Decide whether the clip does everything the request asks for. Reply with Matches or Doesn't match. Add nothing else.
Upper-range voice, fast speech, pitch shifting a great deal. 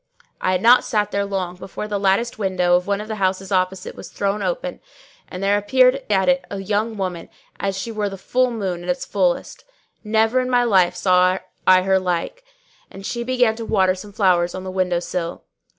Doesn't match